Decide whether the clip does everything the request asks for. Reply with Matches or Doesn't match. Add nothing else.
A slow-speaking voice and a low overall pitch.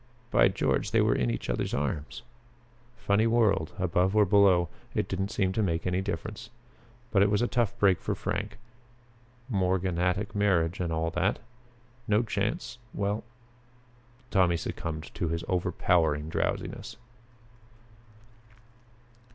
Matches